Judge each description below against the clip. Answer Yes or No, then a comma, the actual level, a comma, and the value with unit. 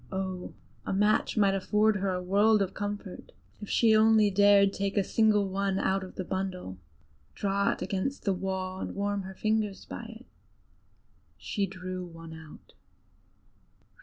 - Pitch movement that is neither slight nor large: No, narrow, 1.7 semitones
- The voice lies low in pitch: No, high, 195 Hz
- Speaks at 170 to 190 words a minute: No, average, 160 wpm